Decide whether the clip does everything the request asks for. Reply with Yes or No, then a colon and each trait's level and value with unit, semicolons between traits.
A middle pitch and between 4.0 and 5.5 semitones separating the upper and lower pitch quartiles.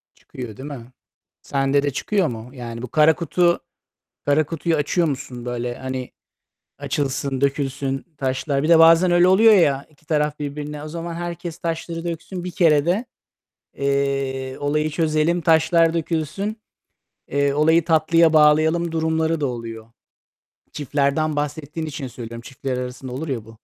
No: medium, 150 Hz; average, 3.5 semitones